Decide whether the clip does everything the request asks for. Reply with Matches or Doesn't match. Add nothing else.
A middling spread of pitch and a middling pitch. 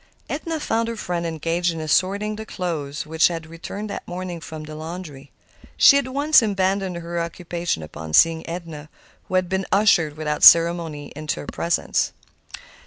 Matches